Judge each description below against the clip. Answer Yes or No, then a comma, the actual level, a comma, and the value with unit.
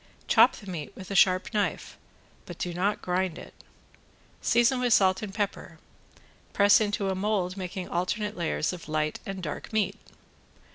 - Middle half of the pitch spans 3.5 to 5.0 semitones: No, narrow, 2.5 semitones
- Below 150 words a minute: No, average, 160 wpm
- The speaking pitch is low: No, high, 190 Hz